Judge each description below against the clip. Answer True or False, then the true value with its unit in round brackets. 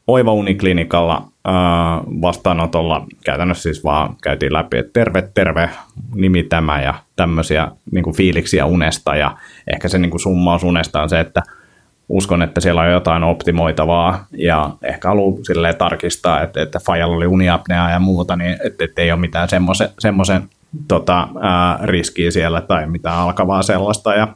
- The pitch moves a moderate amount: False (1.9 semitones)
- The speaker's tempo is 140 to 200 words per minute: True (155 wpm)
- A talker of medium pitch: False (85 Hz)